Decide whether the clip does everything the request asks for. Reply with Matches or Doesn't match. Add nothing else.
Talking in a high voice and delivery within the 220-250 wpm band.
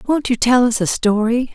Matches